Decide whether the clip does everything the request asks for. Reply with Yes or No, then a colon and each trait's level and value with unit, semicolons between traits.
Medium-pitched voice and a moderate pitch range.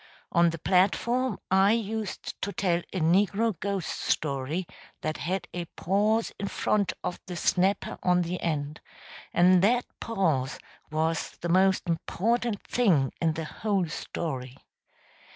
Yes: medium, 180 Hz; average, 3.6 semitones